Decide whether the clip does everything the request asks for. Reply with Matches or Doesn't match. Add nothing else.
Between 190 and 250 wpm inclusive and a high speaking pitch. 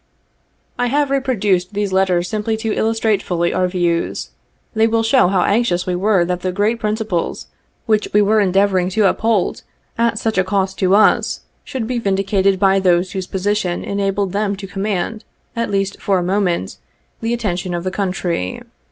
Doesn't match